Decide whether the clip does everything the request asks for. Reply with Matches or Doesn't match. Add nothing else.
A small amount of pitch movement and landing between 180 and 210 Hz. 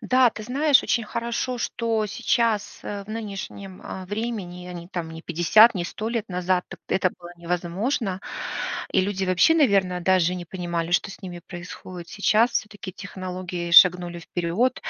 Doesn't match